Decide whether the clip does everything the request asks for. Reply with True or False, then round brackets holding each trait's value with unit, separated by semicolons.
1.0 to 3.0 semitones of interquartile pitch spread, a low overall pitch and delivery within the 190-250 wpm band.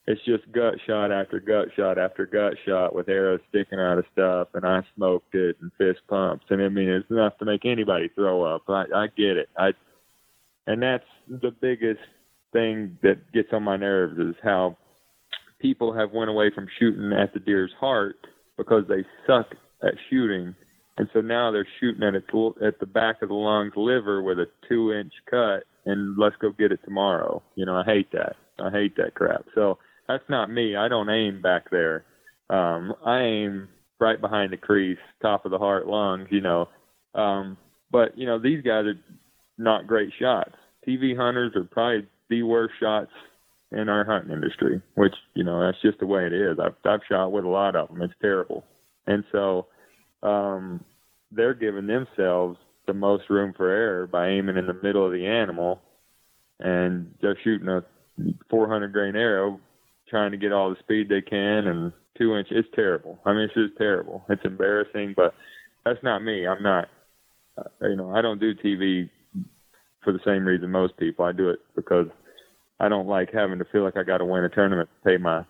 True (2.7 semitones; 100 Hz; 195 wpm)